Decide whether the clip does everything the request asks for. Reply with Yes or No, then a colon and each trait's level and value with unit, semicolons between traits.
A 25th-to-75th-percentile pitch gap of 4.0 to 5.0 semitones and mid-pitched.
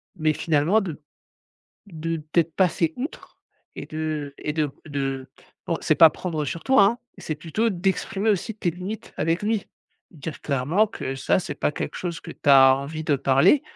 Yes: average, 4.3 semitones; medium, 160 Hz